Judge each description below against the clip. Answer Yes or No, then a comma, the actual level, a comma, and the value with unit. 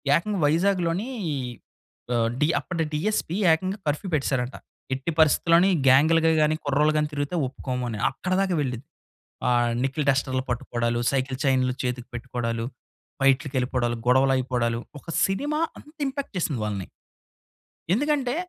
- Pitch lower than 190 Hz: Yes, medium, 140 Hz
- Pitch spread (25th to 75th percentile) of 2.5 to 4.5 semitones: No, average, 5.2 semitones